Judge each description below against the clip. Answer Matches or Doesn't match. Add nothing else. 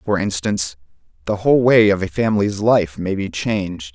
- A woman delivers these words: Doesn't match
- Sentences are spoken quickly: Doesn't match